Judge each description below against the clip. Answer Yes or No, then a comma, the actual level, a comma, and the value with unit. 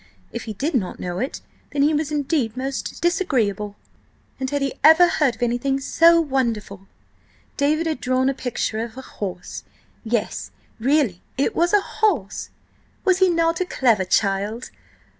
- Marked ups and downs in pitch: Yes, wide, 5.9 semitones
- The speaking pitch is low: No, very high, 265 Hz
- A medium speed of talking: Yes, average, 160 wpm